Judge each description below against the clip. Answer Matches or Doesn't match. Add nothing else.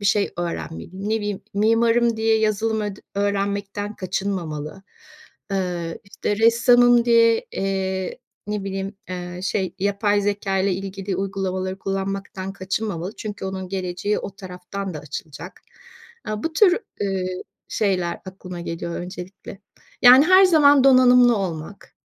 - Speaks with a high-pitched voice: Matches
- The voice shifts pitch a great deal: Doesn't match